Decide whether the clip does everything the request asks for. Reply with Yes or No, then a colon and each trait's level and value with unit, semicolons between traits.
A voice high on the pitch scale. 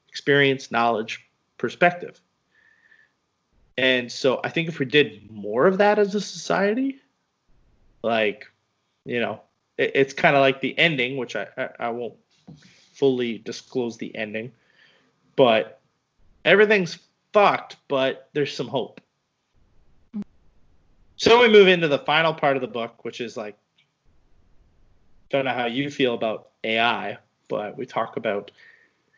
No: low, 135 Hz